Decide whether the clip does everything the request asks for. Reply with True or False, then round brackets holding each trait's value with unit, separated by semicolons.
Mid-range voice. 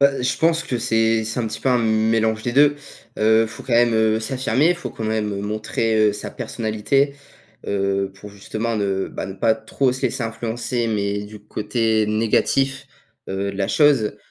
False (110 Hz)